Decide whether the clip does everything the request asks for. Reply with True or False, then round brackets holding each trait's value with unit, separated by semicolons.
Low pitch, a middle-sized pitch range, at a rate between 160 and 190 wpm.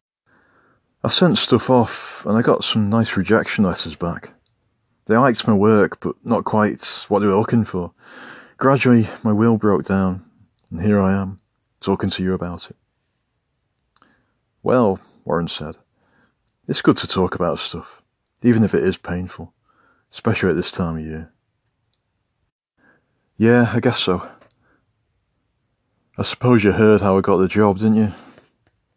False (105 Hz; 3.7 semitones; 150 wpm)